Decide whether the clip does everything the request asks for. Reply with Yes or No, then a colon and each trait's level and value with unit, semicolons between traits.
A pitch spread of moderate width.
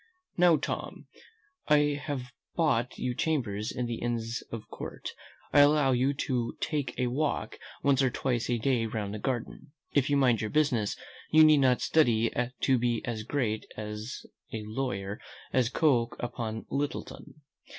Yes: average, 3.8 semitones